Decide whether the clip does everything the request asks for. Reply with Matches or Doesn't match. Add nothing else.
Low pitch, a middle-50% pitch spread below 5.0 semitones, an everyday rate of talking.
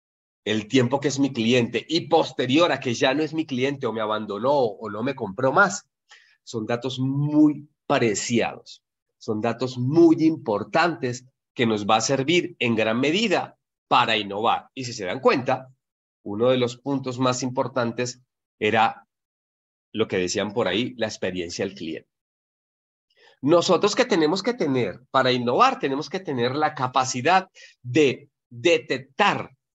Matches